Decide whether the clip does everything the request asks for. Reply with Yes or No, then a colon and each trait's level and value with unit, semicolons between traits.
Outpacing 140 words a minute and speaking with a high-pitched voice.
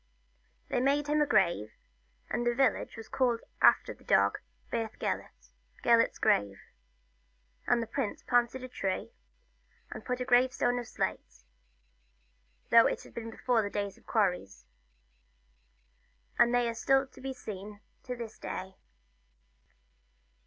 No: slow, 135 wpm; high, 235 Hz